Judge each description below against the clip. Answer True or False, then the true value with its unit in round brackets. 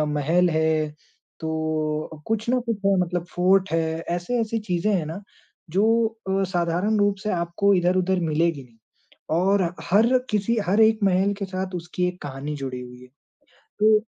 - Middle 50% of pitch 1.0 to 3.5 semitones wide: False (3.9 semitones)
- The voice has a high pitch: False (180 Hz)